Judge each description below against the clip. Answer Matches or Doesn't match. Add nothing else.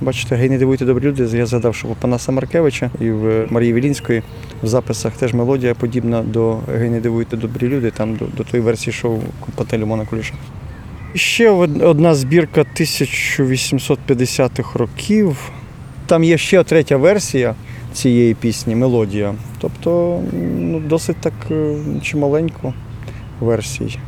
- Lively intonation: Doesn't match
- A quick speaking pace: Doesn't match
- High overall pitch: Doesn't match